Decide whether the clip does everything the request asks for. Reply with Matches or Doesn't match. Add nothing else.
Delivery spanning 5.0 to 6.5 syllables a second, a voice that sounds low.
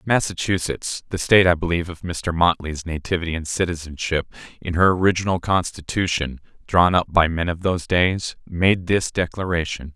Matches